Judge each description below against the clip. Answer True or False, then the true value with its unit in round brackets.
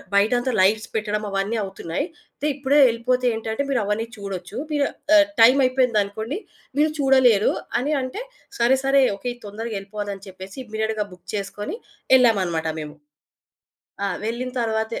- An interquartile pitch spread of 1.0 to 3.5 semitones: False (4.1 semitones)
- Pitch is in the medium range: False (220 Hz)